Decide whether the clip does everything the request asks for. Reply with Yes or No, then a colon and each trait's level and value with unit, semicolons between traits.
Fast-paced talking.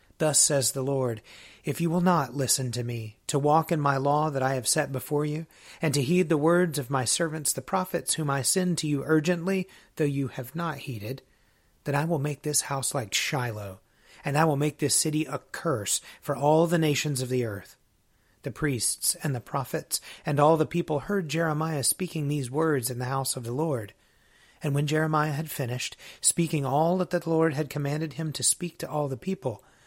Yes: fast, 210 wpm